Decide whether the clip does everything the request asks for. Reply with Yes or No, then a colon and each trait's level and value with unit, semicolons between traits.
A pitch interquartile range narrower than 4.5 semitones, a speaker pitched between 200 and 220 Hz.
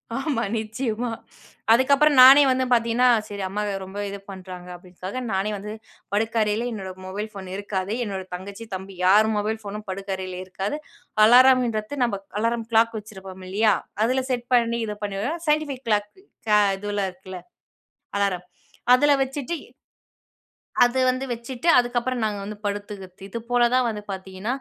Yes: average, 3.9 semitones; high, 215 Hz